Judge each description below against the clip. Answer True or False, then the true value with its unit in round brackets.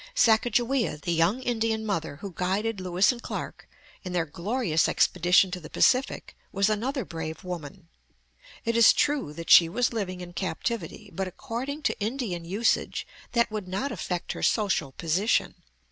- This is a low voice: False (195 Hz)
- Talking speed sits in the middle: True (160 wpm)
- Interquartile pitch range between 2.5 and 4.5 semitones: False (4.9 semitones)